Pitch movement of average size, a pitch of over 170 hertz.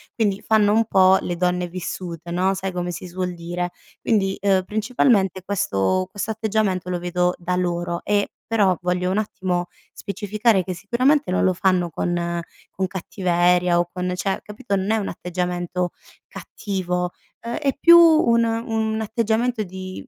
Yes: average, 3.2 semitones; medium, 185 Hz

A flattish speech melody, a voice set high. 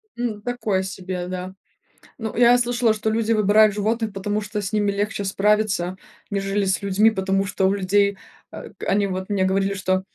Yes: narrow, 2.2 semitones; high, 200 Hz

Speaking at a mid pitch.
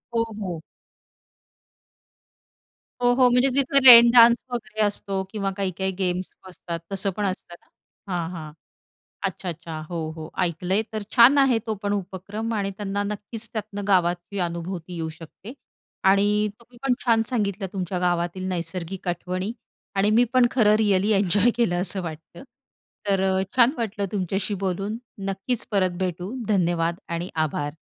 No: high, 195 Hz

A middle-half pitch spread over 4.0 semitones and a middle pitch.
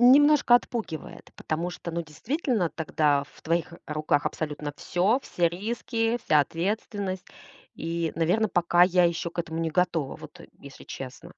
Yes: average, 4.8 semitones; medium, 175 Hz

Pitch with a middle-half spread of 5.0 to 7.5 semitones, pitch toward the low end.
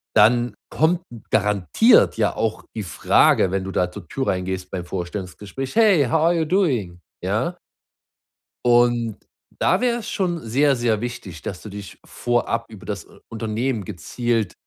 Yes: wide, 5.4 semitones; low, 115 Hz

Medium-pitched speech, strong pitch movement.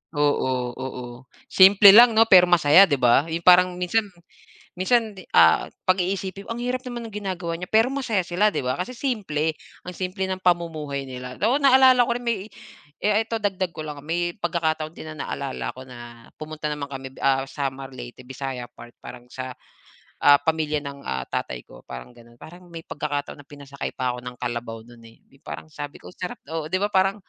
Yes: medium, 160 Hz; wide, 6.3 semitones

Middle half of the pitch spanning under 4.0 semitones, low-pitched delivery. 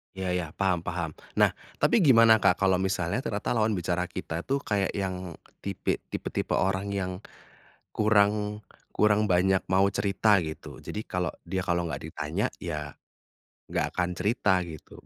Yes: narrow, 2.6 semitones; very low, 95 Hz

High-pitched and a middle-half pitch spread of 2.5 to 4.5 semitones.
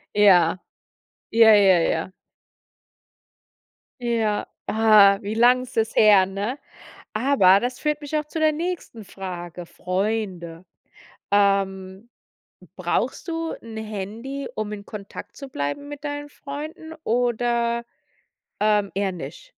No: high, 220 Hz; average, 5.0 semitones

